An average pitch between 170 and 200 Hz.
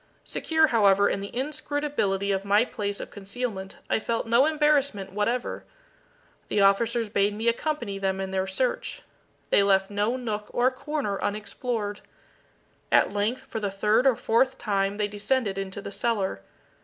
No: high, 210 Hz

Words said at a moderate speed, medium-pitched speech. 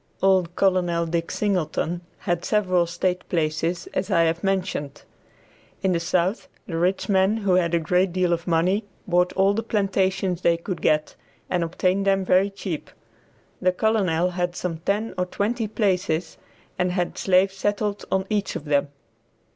Yes: average, 165 wpm; medium, 180 Hz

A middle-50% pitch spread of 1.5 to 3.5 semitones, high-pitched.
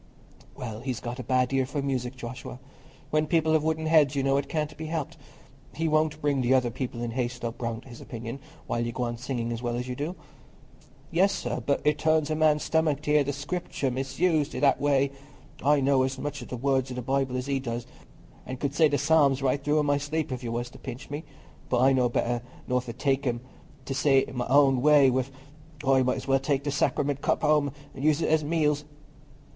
No: average, 2.9 semitones; low, 135 Hz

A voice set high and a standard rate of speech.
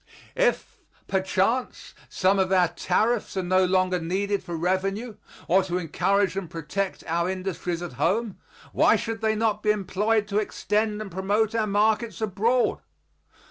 Yes: high, 195 Hz; average, 150 wpm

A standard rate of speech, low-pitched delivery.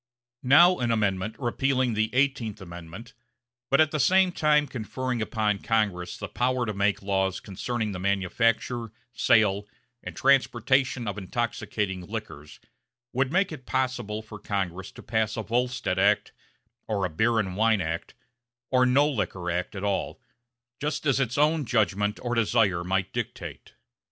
Yes: average, 150 wpm; low, 110 Hz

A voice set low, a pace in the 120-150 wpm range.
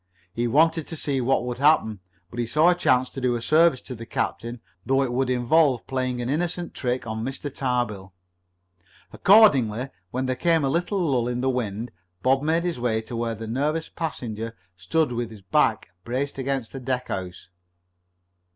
No: low, 130 Hz; average, 185 wpm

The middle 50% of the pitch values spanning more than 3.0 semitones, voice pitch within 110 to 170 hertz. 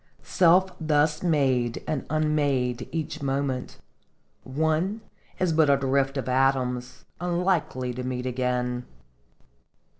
Yes: average, 3.7 semitones; low, 135 Hz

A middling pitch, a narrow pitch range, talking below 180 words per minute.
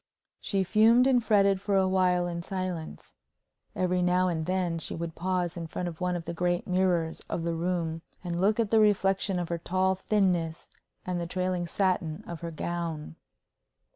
No: medium, 180 Hz; narrow, 1.9 semitones; average, 185 wpm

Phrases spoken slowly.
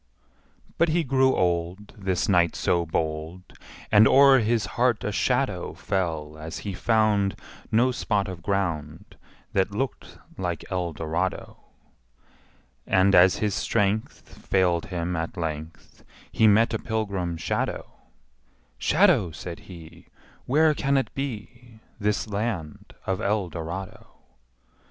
Yes: slow, 120 wpm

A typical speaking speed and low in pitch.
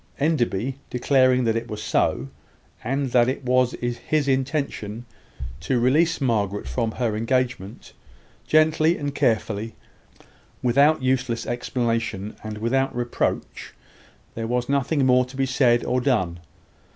No: slow, 125 wpm; low, 125 Hz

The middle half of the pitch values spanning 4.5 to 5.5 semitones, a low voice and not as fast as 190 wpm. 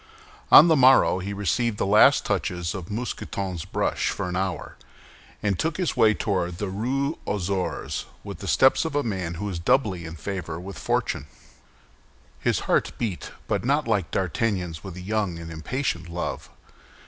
Yes: average, 5.1 semitones; low, 100 Hz; average, 170 wpm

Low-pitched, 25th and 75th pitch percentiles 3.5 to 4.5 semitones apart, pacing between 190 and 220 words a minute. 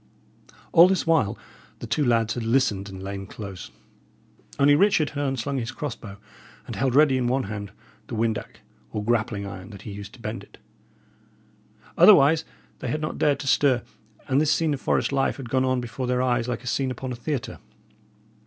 Yes: low, 125 Hz; average, 4.2 semitones; average, 195 wpm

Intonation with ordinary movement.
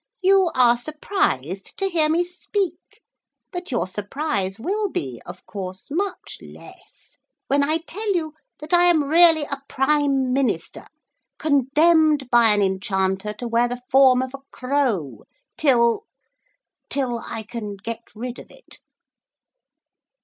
No: wide, 6.1 semitones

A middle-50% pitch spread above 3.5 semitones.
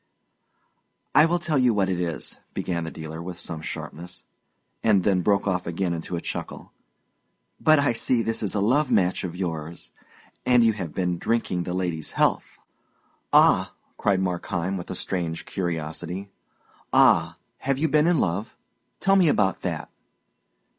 Yes: average, 4.9 semitones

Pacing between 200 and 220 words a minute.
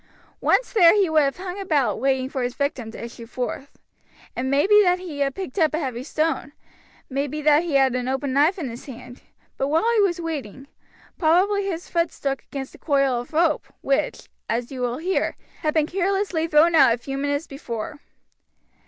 Yes: fast, 205 wpm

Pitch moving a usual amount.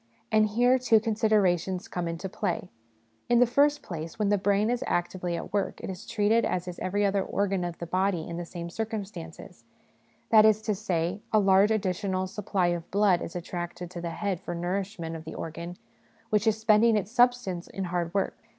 Yes: average, 3.5 semitones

